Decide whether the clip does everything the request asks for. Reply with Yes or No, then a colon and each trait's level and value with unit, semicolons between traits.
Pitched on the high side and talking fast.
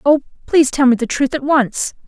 Yes: very high, 275 Hz; fast, 230 wpm